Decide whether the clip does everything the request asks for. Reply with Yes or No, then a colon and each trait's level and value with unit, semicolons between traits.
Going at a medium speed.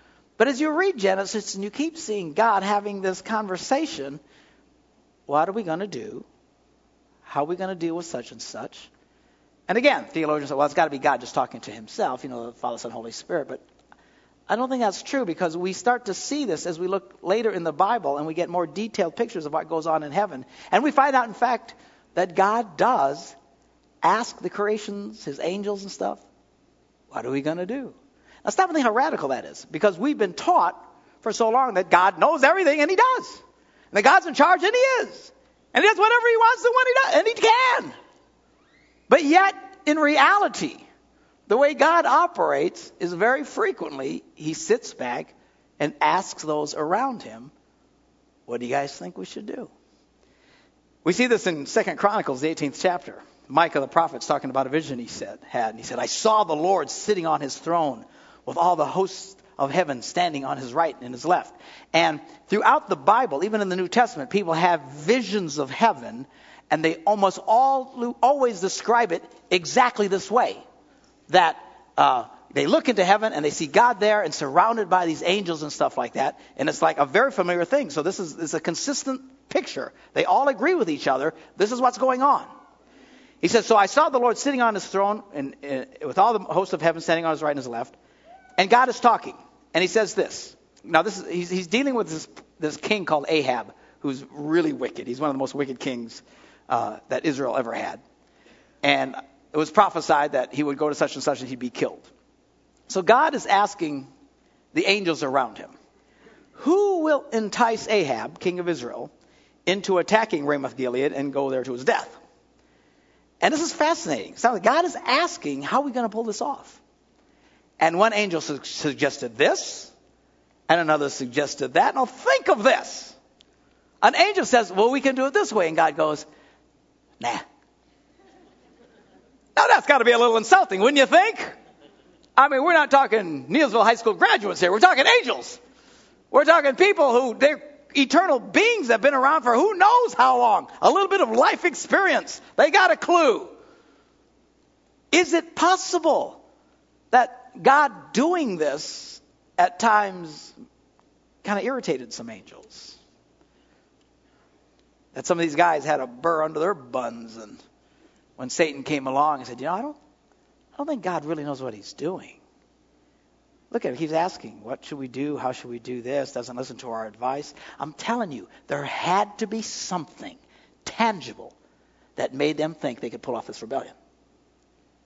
Yes: average, 190 wpm